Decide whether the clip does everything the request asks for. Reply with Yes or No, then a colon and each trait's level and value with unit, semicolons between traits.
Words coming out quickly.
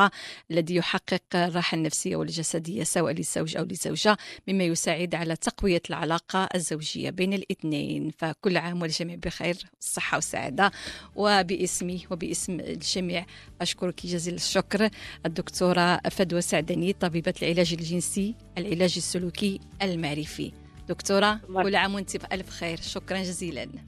No: average, 115 wpm